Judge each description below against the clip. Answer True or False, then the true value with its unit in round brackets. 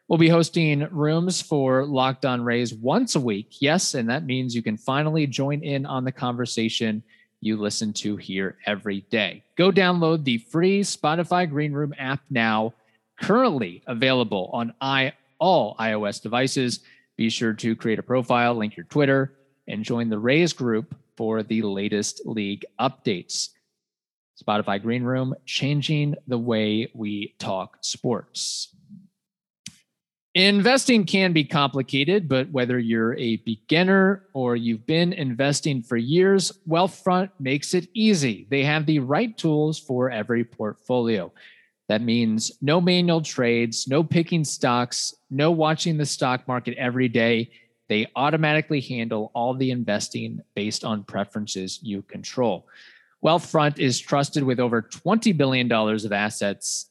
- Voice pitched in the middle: False (130 Hz)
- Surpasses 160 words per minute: False (140 wpm)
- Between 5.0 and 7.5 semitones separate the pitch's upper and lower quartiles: True (5.5 semitones)